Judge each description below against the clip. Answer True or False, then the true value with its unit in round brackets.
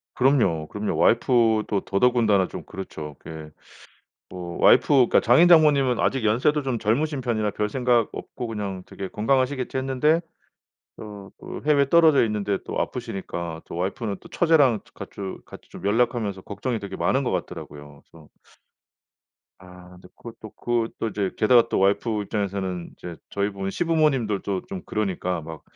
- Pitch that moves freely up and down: False (4.8 semitones)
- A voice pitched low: True (105 Hz)